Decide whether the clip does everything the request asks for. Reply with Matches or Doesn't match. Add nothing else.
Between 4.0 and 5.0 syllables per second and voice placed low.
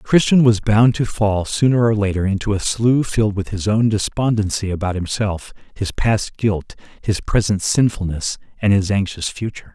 Matches